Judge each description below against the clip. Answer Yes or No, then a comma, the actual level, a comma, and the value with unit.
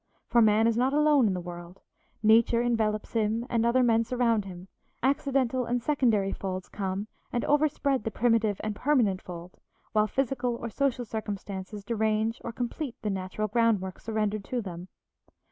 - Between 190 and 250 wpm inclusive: No, average, 160 wpm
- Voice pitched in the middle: No, high, 225 Hz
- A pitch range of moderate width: Yes, average, 3.2 semitones